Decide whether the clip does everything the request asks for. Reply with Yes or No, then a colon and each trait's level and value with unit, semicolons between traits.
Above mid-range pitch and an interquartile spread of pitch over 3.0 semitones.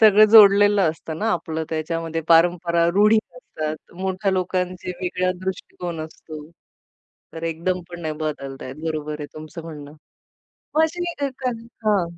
No: medium, 175 Hz; average, 3.7 semitones